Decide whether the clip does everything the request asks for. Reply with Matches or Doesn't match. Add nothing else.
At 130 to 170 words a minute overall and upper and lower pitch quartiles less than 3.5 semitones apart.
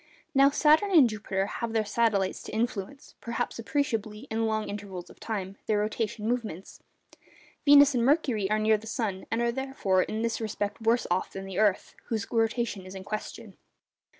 Doesn't match